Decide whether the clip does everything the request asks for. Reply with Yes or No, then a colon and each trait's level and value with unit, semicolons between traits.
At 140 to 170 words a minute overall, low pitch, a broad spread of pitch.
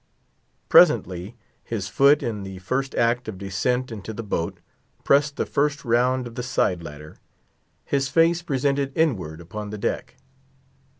Yes: average, 145 wpm; low, 120 Hz; wide, 6.1 semitones